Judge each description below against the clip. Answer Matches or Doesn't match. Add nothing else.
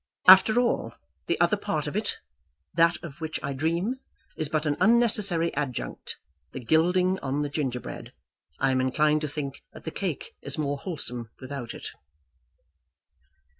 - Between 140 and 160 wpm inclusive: Matches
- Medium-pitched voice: Matches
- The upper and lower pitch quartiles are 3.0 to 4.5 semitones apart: Matches